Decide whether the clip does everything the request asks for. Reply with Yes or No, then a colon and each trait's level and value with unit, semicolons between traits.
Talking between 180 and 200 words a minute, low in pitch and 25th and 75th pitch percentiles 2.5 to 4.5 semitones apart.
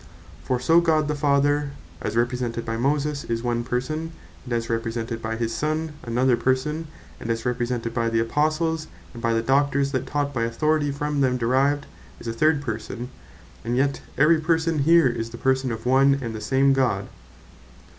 Yes: average, 185 wpm; low, 130 Hz; average, 4.0 semitones